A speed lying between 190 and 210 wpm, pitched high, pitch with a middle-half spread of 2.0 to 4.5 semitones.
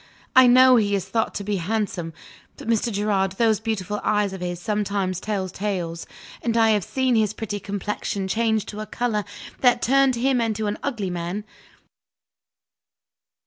No: average, 165 wpm; high, 210 Hz; average, 2.8 semitones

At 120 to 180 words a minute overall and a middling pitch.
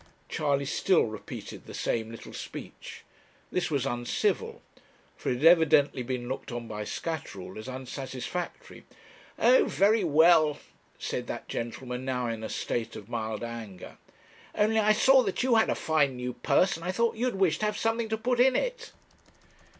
Yes: average, 170 wpm; medium, 150 Hz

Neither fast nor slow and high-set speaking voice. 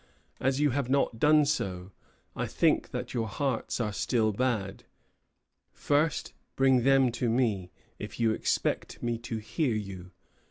No: average, 150 wpm; low, 120 Hz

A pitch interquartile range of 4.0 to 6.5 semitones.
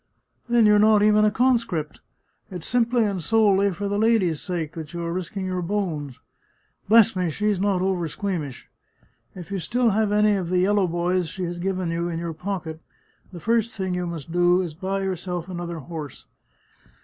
No: average, 3.4 semitones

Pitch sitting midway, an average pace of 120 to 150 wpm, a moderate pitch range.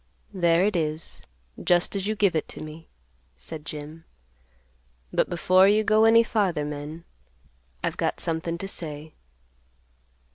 Yes: medium, 170 Hz; average, 140 wpm; average, 4.1 semitones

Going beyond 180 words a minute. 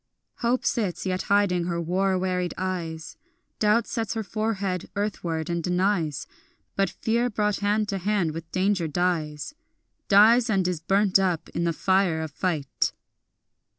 No: average, 150 wpm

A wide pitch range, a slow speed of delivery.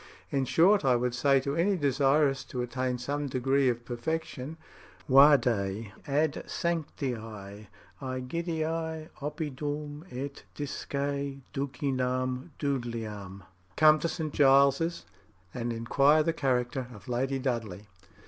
No: average, 3.1 semitones; slow, 110 wpm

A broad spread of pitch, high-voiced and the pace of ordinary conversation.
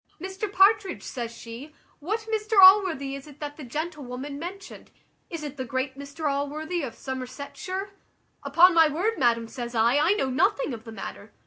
Yes: wide, 5.7 semitones; very high, 290 Hz; average, 175 wpm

